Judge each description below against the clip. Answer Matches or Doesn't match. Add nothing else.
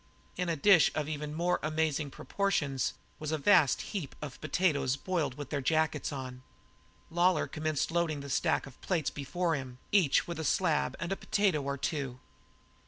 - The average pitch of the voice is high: Doesn't match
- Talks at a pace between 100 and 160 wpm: Doesn't match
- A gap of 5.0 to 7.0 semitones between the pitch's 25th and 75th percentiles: Doesn't match